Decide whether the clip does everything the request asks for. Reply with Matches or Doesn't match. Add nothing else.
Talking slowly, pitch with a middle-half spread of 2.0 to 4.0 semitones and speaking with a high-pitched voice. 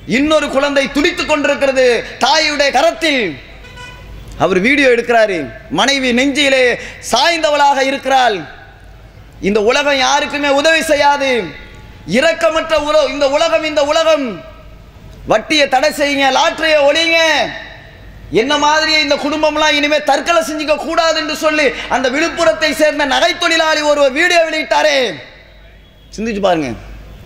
Matches